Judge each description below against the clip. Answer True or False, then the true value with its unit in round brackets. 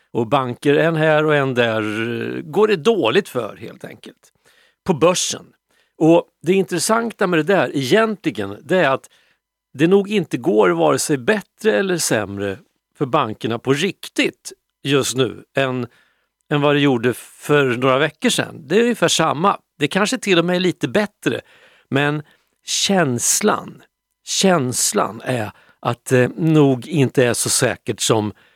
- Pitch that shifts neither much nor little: False (6.4 semitones)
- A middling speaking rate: True (155 wpm)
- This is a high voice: False (150 Hz)